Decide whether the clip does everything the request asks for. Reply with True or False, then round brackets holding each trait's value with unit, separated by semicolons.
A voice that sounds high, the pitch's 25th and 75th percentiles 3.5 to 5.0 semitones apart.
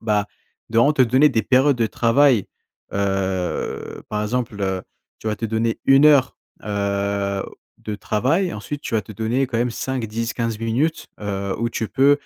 False (115 Hz; 4.1 semitones)